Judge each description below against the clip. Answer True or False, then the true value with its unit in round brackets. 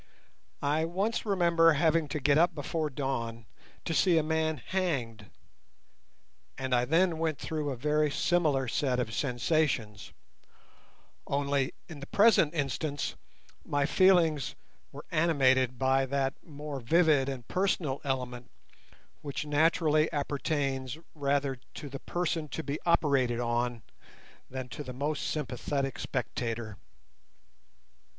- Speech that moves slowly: True (125 wpm)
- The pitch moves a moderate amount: True (3.4 semitones)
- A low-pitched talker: False (145 Hz)